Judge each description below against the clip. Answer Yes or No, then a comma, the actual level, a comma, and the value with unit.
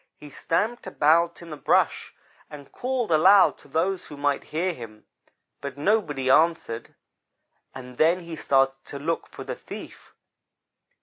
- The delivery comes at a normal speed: Yes, average, 145 wpm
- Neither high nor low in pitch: Yes, medium, 155 Hz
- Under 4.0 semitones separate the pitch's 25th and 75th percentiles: No, average, 4.3 semitones